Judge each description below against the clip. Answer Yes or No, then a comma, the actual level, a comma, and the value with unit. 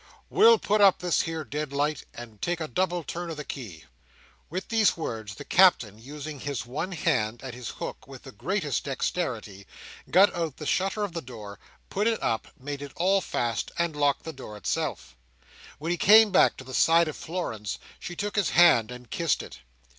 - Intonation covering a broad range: Yes, wide, 6.5 semitones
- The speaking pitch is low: No, medium, 155 Hz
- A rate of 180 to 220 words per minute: Yes, average, 195 wpm